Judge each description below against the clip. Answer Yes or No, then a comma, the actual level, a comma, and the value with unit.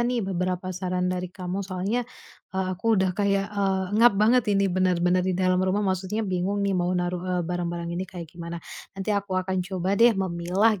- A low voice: No, medium, 185 Hz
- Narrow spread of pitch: Yes, narrow, 1.8 semitones